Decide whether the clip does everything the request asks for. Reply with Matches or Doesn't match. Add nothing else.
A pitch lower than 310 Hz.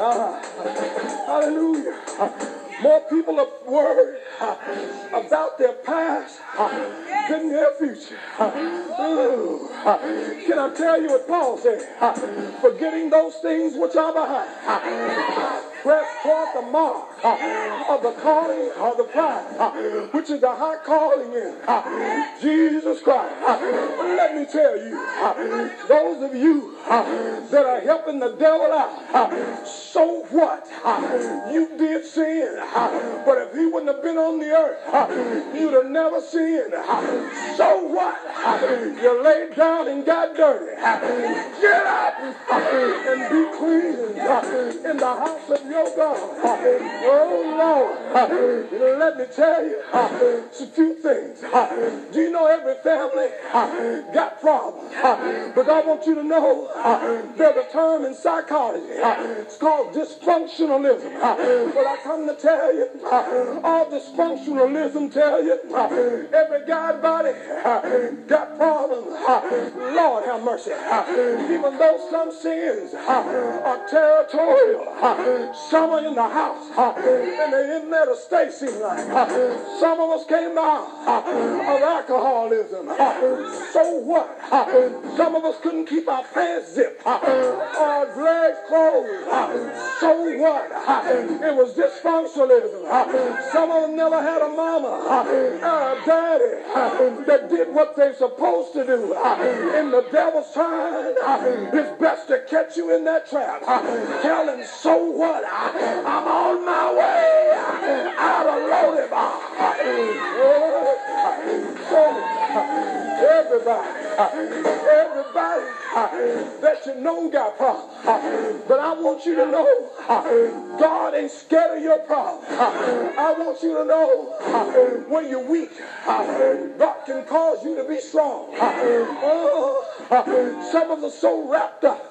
Doesn't match